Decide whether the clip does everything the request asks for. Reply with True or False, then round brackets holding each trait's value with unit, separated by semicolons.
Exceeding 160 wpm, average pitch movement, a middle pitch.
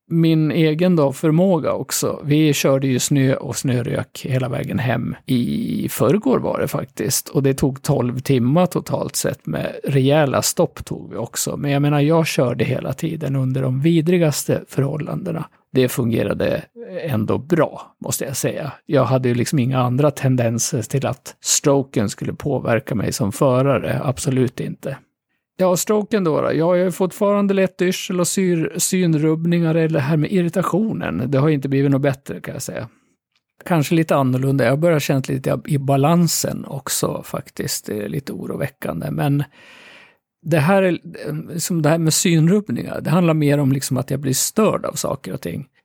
True (170 wpm; 4.0 semitones; 150 Hz)